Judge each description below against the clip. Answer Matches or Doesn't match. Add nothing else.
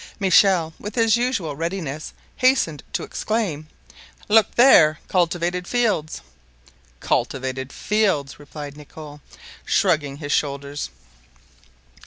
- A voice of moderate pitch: Matches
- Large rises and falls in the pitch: Matches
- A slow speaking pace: Matches